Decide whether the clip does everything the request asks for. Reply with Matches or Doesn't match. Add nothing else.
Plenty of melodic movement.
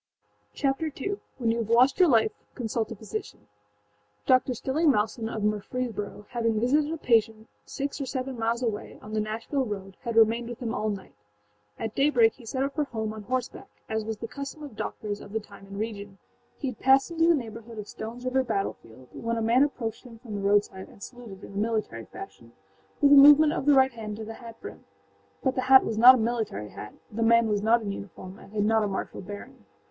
Doesn't match